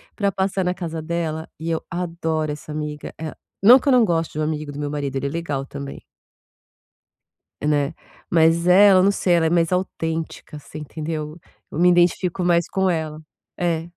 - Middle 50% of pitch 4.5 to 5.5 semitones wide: No, average, 2.7 semitones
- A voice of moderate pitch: Yes, medium, 165 Hz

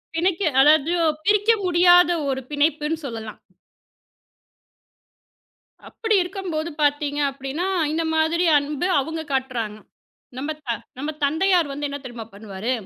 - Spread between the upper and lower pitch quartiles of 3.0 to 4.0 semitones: No, average, 4.4 semitones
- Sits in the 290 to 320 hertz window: Yes, very high, 300 Hz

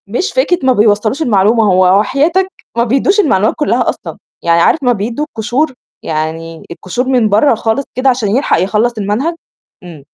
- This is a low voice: No, high, 225 Hz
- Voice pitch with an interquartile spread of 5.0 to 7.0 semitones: Yes, wide, 5.6 semitones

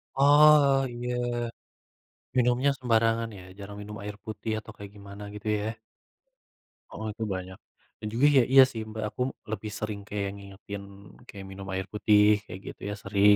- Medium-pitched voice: No, low, 105 Hz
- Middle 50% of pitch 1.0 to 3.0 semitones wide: Yes, average, 2.7 semitones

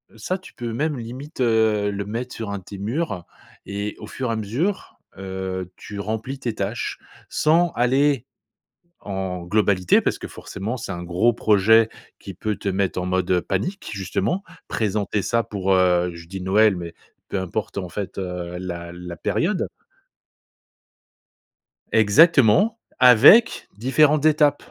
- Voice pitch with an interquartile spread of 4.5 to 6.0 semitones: Yes, average, 4.9 semitones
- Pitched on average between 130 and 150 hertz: No, low, 105 Hz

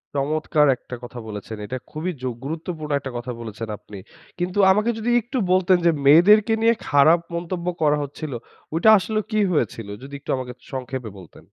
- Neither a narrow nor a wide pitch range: No, wide, 6.1 semitones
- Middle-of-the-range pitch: Yes, medium, 150 Hz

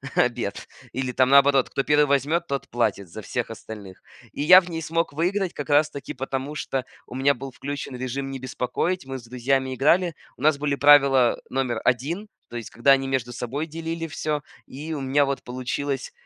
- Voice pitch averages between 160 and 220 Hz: No, low, 135 Hz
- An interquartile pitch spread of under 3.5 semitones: Yes, average, 2.8 semitones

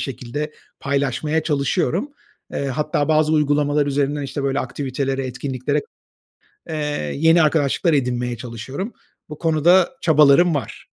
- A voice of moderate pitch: Yes, medium, 145 Hz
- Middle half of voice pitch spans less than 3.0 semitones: Yes, narrow, 2.6 semitones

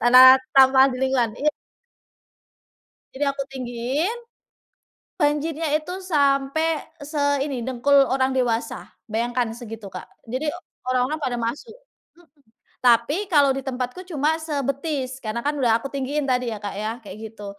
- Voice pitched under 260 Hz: No, very high, 265 Hz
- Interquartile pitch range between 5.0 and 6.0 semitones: No, average, 3.3 semitones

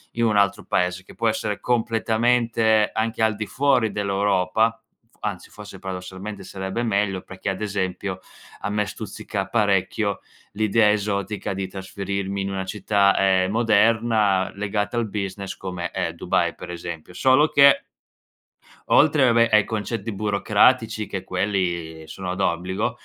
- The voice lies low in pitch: Yes, low, 100 Hz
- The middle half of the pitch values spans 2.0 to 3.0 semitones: Yes, narrow, 2.6 semitones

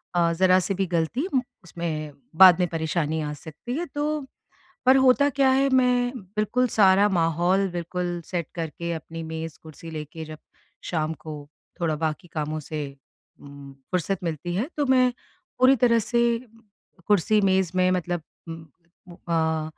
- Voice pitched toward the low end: No, medium, 175 Hz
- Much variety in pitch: Yes, wide, 6.3 semitones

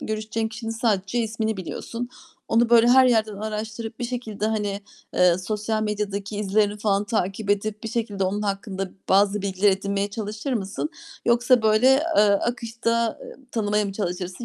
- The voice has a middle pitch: No, high, 215 Hz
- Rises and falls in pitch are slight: Yes, narrow, 2.2 semitones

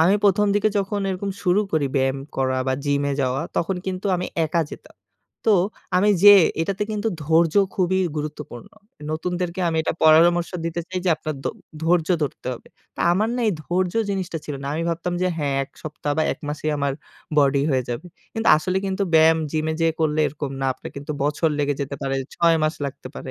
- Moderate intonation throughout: Yes, average, 4.1 semitones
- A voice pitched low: No, medium, 160 Hz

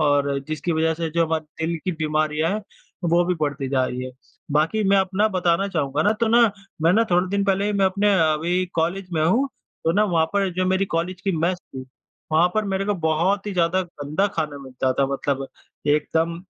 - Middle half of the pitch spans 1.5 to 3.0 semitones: No, average, 3.7 semitones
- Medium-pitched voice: Yes, medium, 170 Hz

